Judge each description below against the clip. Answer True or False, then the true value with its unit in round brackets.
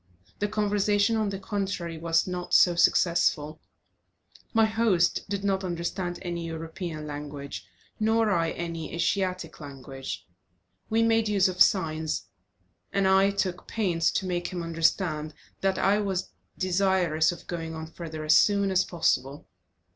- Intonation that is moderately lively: True (3.5 semitones)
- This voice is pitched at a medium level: True (180 Hz)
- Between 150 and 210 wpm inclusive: False (140 wpm)